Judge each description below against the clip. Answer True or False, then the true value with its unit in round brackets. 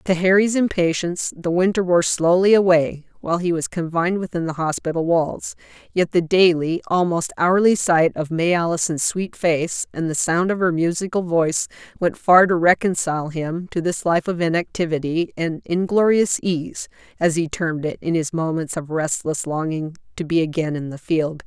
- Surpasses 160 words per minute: True (175 wpm)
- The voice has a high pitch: False (170 Hz)